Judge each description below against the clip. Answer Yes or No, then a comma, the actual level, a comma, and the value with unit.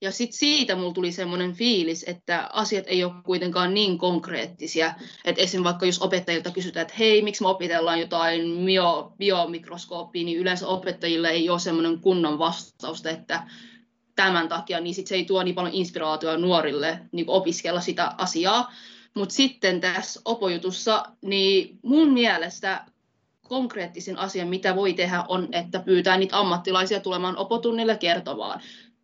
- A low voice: No, medium, 185 Hz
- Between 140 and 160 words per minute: Yes, average, 145 wpm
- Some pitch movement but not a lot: No, narrow, 2.1 semitones